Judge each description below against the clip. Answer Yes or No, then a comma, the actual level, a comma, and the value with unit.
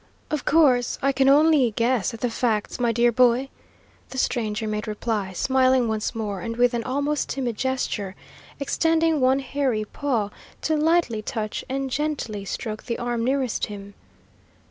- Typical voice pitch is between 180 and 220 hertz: No, high, 245 Hz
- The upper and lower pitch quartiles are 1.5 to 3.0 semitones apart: No, average, 3.8 semitones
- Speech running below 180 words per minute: Yes, average, 160 wpm